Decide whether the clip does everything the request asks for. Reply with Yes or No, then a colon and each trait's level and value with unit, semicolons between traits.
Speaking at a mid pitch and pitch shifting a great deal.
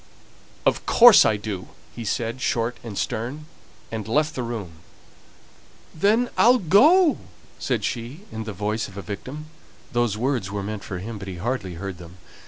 No: low, 115 Hz; wide, 6.5 semitones